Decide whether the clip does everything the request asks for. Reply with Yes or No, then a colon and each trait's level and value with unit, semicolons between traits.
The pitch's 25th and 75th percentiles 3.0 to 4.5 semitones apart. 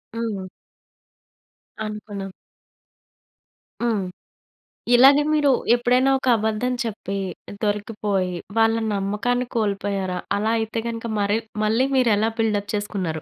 No: narrow, 2.5 semitones